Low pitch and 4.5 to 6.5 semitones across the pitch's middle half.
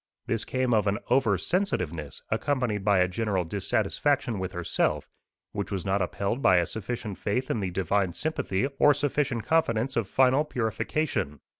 Yes: low, 105 Hz; average, 5.3 semitones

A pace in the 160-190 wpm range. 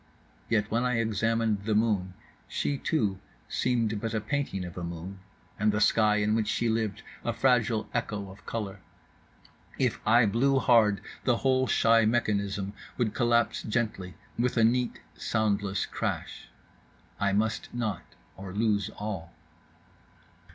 No: average, 145 wpm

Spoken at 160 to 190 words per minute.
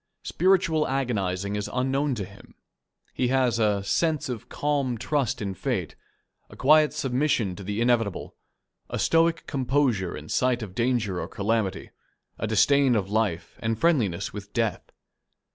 No: average, 145 wpm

